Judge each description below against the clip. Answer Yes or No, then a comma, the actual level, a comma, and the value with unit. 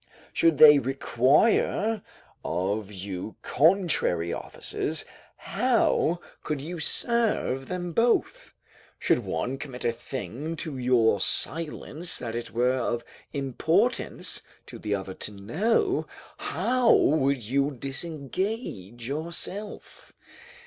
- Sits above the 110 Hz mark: Yes, medium, 140 Hz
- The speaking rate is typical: No, slow, 105 wpm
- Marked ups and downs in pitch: Yes, wide, 6.7 semitones